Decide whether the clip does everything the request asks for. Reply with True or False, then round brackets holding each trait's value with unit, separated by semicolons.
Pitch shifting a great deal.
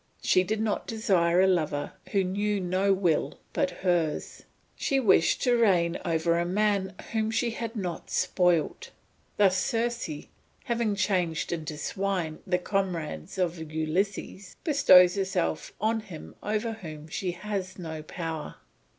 False (3.7 semitones)